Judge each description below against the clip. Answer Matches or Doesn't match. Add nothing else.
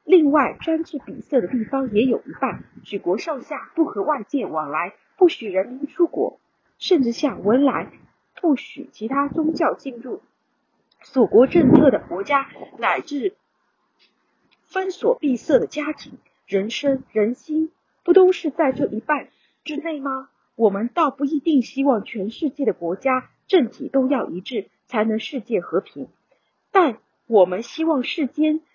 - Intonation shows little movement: Doesn't match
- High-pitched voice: Matches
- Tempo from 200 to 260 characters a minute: Matches